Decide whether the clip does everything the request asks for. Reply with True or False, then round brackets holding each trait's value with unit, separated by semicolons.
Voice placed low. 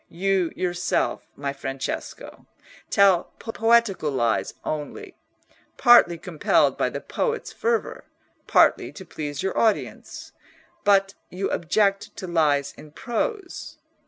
False (185 Hz)